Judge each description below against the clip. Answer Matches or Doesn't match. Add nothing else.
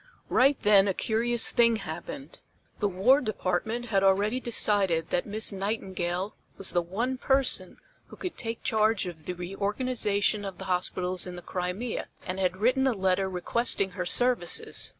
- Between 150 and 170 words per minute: Matches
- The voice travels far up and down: Doesn't match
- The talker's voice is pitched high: Matches